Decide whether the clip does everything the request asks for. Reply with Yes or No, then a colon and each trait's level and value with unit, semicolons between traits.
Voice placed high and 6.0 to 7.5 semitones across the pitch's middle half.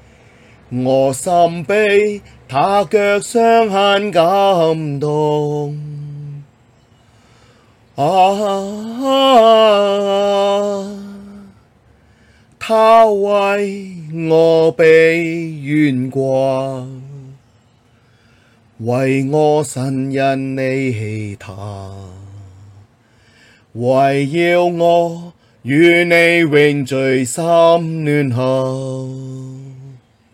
No: medium, 145 Hz; wide, 6.4 semitones